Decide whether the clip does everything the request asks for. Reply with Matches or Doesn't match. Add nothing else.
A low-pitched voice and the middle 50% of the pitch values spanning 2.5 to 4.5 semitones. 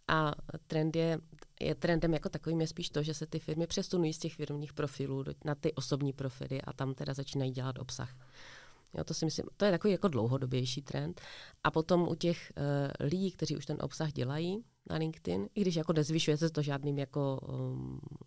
Doesn't match